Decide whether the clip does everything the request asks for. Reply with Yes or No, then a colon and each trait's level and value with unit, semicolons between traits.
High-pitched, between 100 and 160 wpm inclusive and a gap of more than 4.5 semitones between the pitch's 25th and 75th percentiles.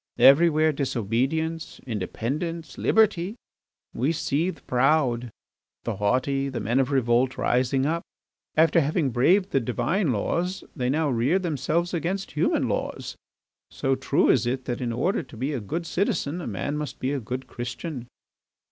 No: medium, 140 Hz; average, 155 wpm; average, 4.9 semitones